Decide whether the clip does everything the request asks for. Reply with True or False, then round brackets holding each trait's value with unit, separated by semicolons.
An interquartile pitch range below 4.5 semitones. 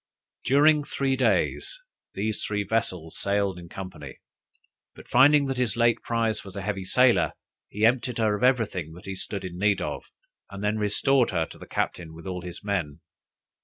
False (4.8 semitones)